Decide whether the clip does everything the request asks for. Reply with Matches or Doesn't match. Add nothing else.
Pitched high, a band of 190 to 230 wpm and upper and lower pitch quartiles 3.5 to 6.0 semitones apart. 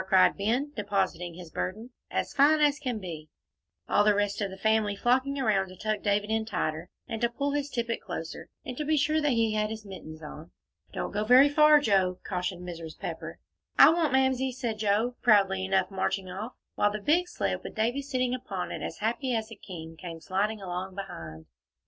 Matches